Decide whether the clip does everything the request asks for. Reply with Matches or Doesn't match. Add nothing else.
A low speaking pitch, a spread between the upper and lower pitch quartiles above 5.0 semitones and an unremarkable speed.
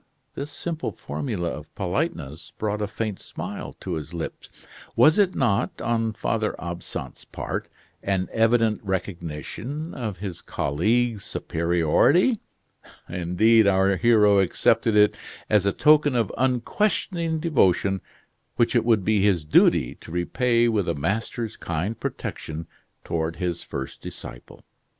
Doesn't match